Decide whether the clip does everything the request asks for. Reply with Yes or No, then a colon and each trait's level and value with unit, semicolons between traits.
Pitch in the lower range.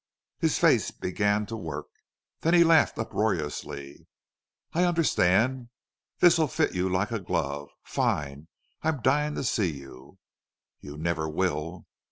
Yes: very low, 95 Hz